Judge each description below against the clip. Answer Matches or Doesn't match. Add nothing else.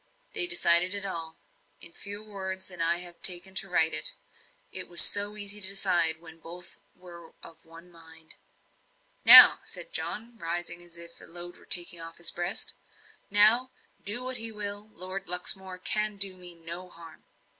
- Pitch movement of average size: Matches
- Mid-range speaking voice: Matches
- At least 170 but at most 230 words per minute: Matches